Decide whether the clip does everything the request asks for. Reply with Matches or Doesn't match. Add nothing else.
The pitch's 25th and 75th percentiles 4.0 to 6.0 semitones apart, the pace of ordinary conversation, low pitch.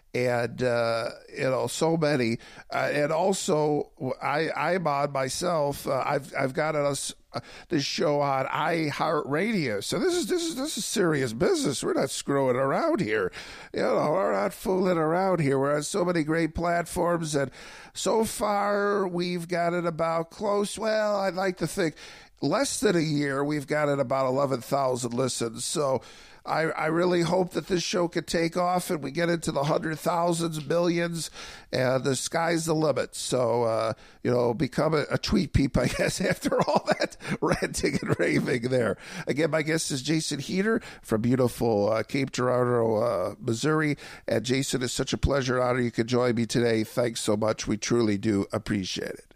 Doesn't match